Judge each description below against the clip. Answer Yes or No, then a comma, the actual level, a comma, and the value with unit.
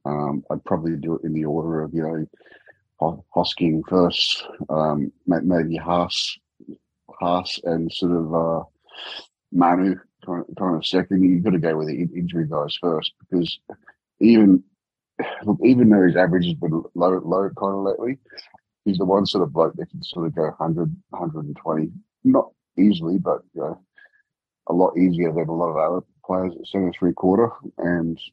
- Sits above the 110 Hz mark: No, very low, 85 Hz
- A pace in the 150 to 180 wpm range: Yes, average, 170 wpm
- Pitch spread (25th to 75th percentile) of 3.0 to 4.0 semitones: No, narrow, 2.5 semitones